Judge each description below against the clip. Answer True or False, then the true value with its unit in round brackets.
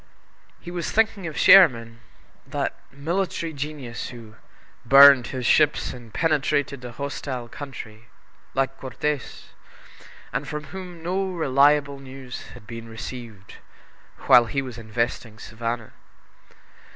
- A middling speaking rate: False (115 wpm)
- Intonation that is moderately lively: True (4.3 semitones)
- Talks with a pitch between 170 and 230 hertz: False (135 Hz)